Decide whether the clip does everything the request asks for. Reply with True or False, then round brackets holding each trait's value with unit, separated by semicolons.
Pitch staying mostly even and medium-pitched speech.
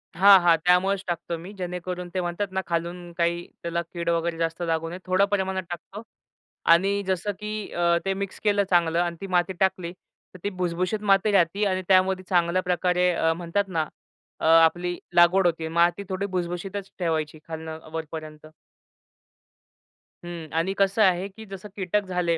True (2.2 semitones; 180 Hz)